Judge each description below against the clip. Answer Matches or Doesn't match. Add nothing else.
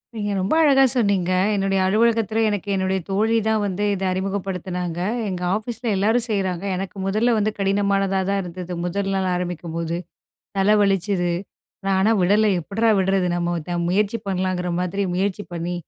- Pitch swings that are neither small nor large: Doesn't match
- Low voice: Doesn't match